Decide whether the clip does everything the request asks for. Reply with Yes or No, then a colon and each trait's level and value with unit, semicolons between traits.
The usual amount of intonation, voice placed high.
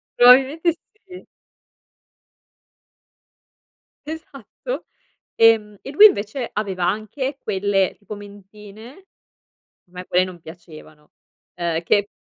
No: wide, 6.4 semitones; high, 210 Hz